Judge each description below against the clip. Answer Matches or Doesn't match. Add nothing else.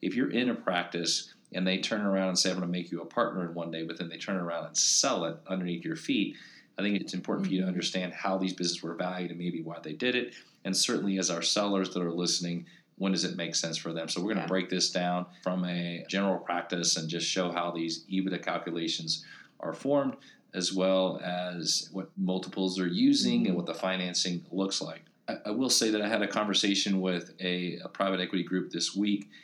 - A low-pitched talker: Matches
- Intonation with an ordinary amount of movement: Doesn't match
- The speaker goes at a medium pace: Doesn't match